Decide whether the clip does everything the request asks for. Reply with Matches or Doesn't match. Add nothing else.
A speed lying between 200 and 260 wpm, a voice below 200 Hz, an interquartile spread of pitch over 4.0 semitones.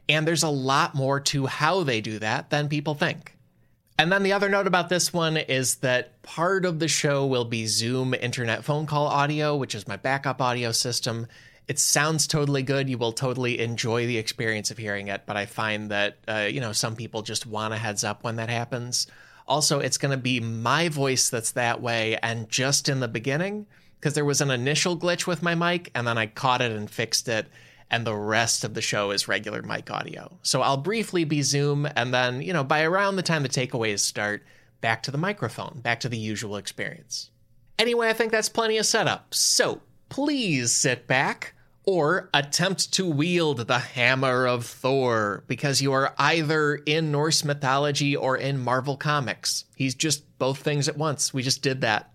Matches